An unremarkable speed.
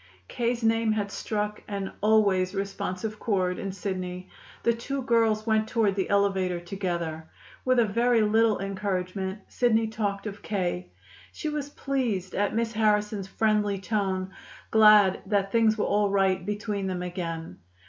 Yes: average, 150 wpm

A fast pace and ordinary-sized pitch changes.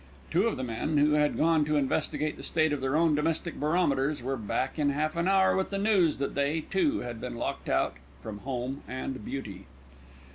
Yes: fast, 210 wpm; average, 3.6 semitones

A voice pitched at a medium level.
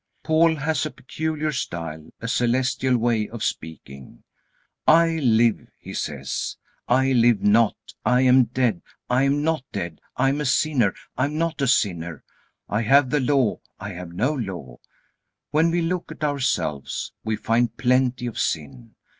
No: low, 125 Hz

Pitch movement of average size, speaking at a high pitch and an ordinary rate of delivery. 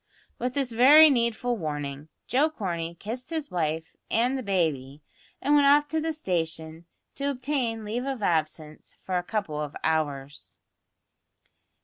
No: wide, 8.8 semitones; high, 210 Hz; average, 145 wpm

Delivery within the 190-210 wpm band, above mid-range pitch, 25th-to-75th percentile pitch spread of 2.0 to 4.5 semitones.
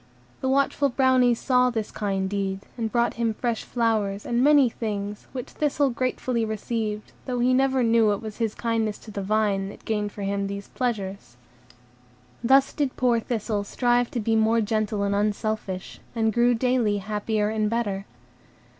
No: average, 170 wpm; high, 225 Hz; average, 2.9 semitones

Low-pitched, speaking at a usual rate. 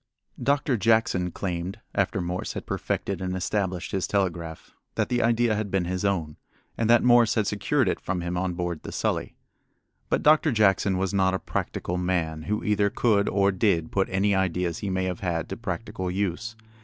Yes: very low, 95 Hz; average, 190 wpm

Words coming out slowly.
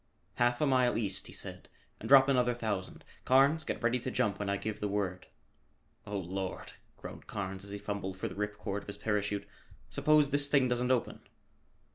No: average, 195 wpm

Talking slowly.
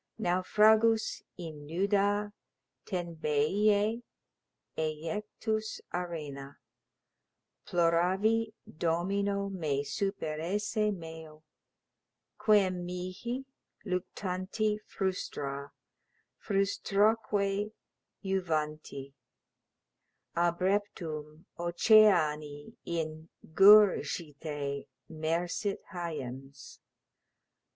Yes: slow, 50 wpm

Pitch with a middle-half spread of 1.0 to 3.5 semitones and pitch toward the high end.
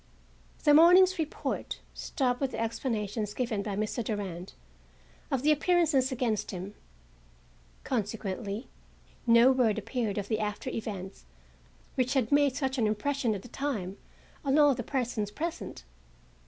No: average, 4.7 semitones; high, 240 Hz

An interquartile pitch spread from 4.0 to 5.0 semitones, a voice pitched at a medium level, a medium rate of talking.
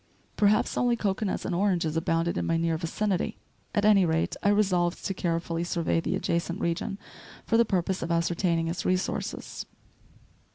No: average, 3.1 semitones; medium, 175 Hz; average, 160 wpm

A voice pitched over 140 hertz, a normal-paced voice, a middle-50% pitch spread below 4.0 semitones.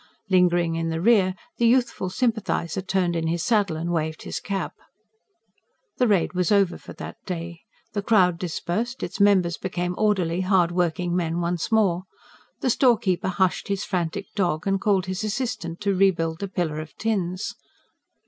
Yes: medium, 185 Hz; average, 165 wpm; average, 2.9 semitones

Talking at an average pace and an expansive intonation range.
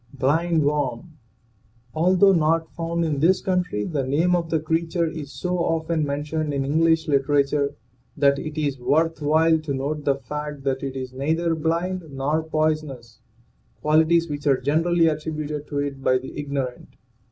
No: average, 160 wpm; narrow, 2.6 semitones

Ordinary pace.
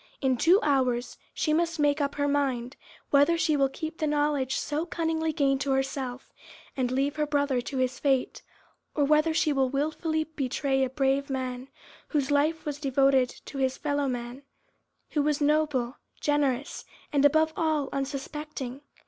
Yes: average, 165 wpm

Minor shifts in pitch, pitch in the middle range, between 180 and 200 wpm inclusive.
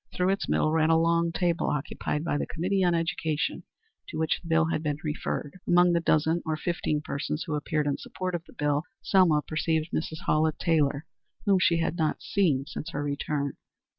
Yes: narrow, 2.1 semitones; medium, 160 Hz; average, 195 wpm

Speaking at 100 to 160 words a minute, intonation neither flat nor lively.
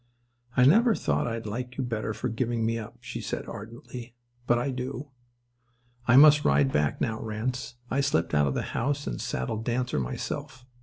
No: average, 185 wpm; average, 3.0 semitones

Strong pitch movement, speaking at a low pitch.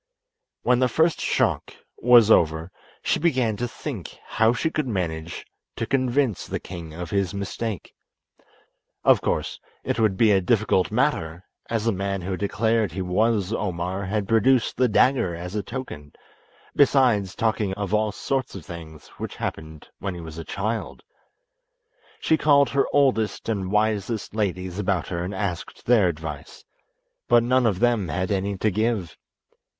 No: average, 4.4 semitones; low, 105 Hz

